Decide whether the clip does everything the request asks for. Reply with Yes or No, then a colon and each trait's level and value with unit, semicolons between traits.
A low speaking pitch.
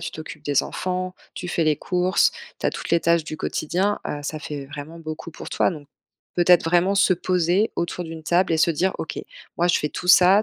No: medium, 170 Hz